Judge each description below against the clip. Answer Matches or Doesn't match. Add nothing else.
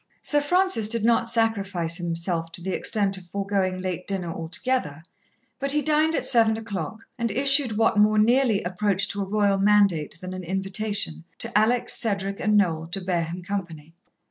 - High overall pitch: Matches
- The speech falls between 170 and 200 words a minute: Matches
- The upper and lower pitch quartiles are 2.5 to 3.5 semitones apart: Doesn't match